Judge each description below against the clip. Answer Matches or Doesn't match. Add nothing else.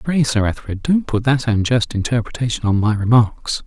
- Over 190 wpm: Doesn't match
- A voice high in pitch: Doesn't match